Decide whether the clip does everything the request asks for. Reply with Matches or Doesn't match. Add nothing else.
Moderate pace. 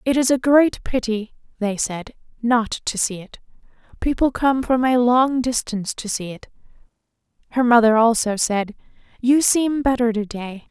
Matches